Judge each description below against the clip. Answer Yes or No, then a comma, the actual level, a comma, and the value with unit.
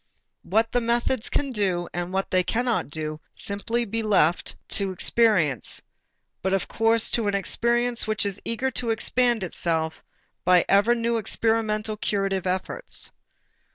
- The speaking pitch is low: No, high, 215 Hz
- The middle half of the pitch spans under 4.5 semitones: Yes, average, 3.7 semitones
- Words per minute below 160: Yes, average, 150 wpm